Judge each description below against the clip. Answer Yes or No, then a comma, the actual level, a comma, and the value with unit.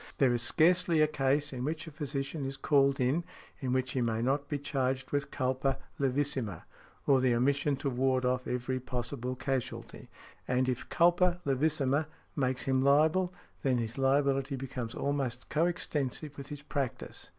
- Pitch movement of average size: No, narrow, 2.3 semitones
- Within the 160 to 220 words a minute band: Yes, average, 165 wpm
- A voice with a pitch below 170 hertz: Yes, low, 135 Hz